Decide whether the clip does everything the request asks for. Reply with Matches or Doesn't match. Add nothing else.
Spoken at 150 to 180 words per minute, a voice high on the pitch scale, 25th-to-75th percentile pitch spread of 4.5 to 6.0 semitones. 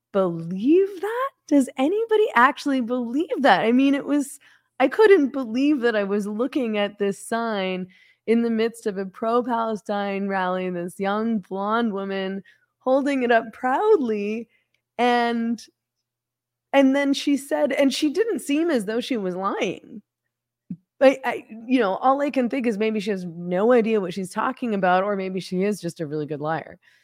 Matches